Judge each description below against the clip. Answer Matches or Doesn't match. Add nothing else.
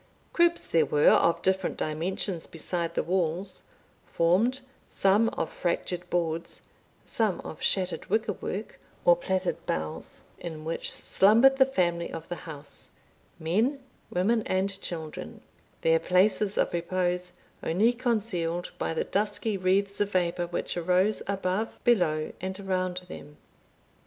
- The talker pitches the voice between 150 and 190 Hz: Matches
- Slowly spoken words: Matches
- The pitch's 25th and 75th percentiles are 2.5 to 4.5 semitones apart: Matches